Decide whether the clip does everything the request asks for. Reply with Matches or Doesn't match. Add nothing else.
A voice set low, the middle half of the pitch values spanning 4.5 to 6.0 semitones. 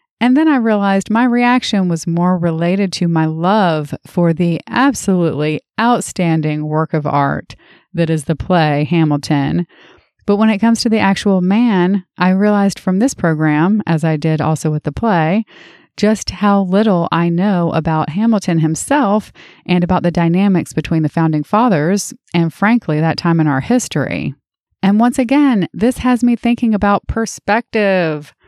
Doesn't match